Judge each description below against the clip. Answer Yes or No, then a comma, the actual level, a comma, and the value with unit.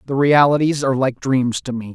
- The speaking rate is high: Yes, fast, 215 wpm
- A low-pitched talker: Yes, low, 130 Hz